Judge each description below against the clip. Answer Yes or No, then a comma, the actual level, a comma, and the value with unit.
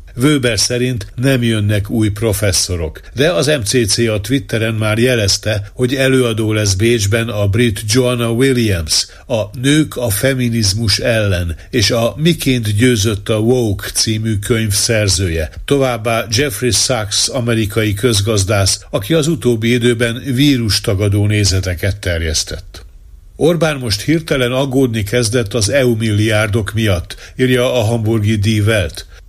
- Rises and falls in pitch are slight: No, average, 3.4 semitones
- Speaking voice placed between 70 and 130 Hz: Yes, low, 115 Hz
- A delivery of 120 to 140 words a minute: Yes, average, 125 wpm